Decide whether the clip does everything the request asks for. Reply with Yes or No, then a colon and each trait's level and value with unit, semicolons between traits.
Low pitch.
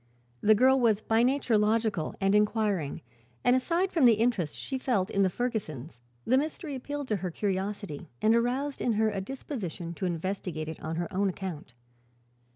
No: high, 210 Hz